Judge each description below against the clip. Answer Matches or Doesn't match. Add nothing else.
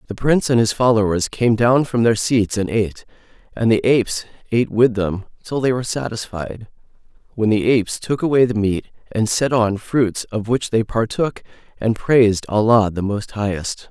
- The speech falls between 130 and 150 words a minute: Doesn't match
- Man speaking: Matches